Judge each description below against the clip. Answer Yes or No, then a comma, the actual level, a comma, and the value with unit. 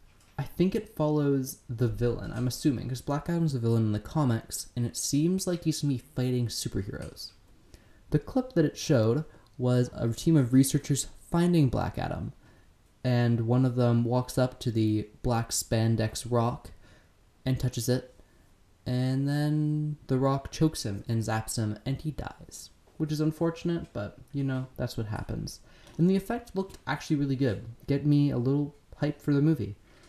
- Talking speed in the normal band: Yes, average, 175 wpm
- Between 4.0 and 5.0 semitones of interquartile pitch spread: Yes, average, 4.6 semitones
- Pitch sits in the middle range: No, low, 125 Hz